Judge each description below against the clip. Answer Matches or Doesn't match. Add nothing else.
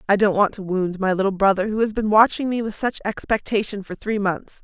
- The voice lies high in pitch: Matches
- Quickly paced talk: Matches